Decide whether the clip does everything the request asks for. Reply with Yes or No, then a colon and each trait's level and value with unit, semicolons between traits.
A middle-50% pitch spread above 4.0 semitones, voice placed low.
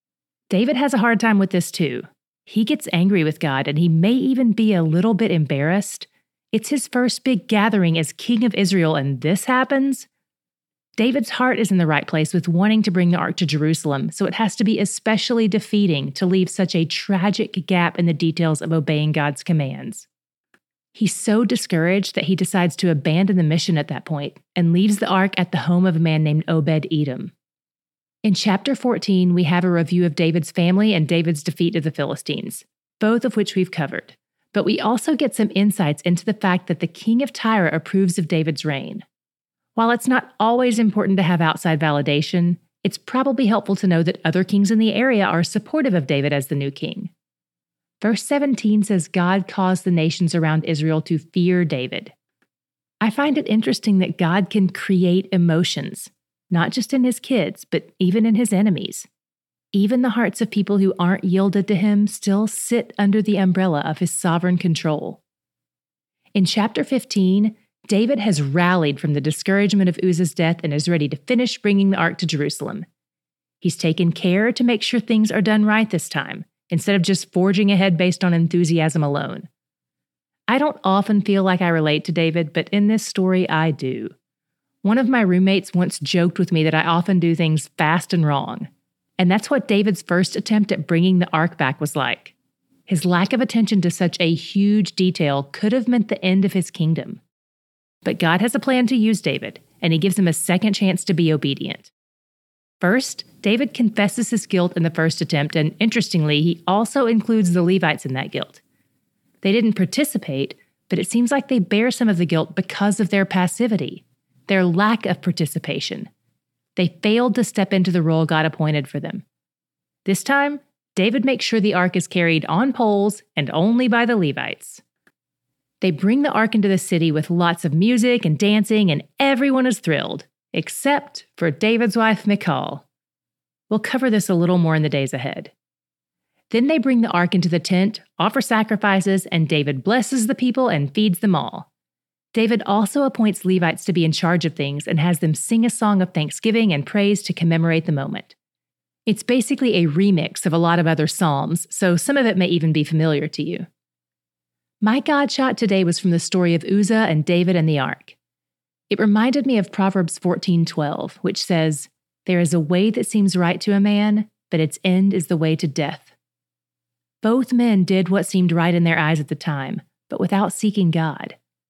No: average, 4.6 semitones; medium, 185 Hz